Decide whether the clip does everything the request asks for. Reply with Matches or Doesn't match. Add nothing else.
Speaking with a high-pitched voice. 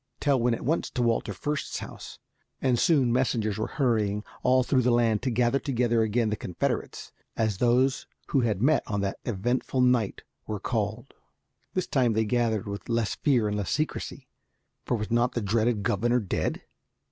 Doesn't match